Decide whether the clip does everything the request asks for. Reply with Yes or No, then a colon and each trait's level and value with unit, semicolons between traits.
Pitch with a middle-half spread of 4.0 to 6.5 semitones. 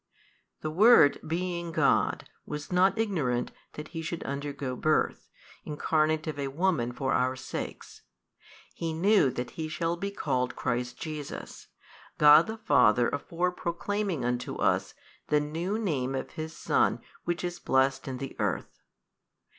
Yes: average, 4.5 semitones